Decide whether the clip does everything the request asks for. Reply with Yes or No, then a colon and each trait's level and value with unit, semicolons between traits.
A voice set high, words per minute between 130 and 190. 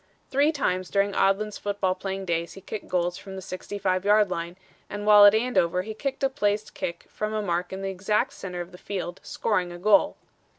No: high, 195 Hz; fast, 205 wpm